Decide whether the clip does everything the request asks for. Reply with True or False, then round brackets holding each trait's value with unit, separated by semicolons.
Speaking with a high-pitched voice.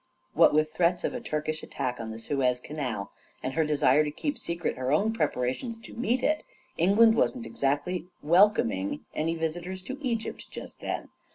False (160 Hz)